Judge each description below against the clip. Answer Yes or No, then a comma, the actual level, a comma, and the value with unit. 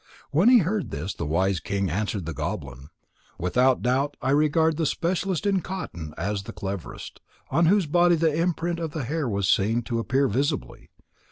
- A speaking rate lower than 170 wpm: No, average, 180 wpm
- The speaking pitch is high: No, low, 135 Hz